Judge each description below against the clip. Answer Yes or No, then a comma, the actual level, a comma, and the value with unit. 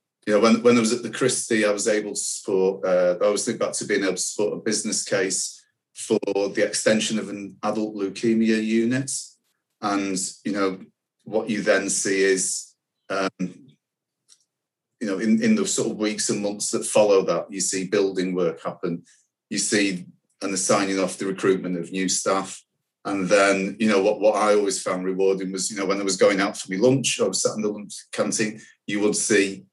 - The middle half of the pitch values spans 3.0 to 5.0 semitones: No, narrow, 2.4 semitones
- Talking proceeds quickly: Yes, fast, 210 wpm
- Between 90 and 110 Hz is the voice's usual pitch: Yes, low, 100 Hz